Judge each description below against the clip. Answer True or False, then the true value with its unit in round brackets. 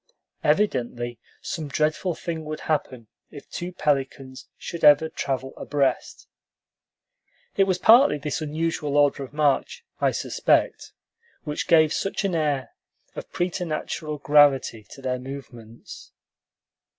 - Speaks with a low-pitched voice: False (150 Hz)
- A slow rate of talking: True (120 wpm)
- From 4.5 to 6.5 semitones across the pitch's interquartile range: False (3.2 semitones)